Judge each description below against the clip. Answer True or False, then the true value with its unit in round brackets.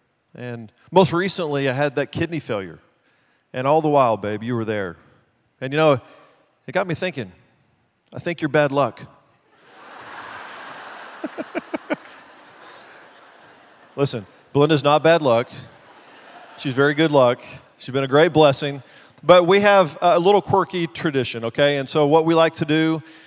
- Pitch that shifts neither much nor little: True (4.1 semitones)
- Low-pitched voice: False (145 Hz)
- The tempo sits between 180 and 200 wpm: False (145 wpm)